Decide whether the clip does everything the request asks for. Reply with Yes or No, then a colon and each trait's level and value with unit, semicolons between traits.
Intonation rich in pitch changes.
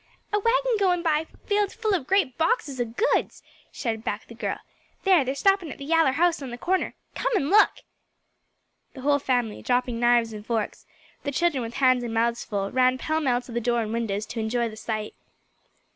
Yes: wide, 6.7 semitones